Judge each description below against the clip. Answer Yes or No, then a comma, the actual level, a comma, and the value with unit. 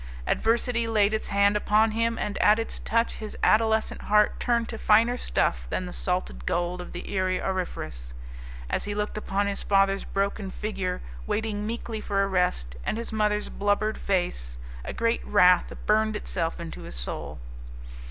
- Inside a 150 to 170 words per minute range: Yes, average, 165 wpm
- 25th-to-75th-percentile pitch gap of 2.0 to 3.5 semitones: Yes, average, 3.2 semitones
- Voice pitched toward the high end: Yes, high, 205 Hz